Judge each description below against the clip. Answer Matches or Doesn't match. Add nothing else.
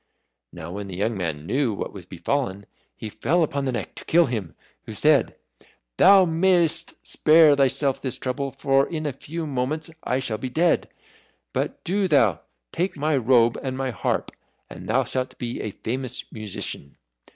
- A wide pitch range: Matches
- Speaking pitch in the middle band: Doesn't match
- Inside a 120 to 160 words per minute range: Doesn't match